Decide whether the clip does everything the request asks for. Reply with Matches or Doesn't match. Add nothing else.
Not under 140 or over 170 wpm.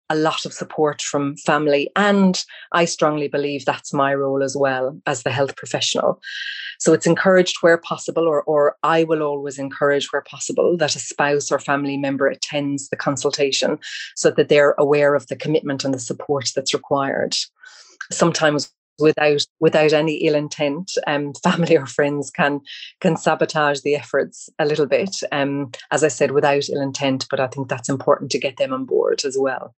Doesn't match